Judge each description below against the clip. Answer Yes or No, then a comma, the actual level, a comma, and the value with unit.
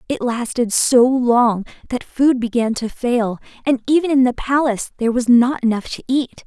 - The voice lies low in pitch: No, high, 245 Hz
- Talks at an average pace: Yes, average, 185 wpm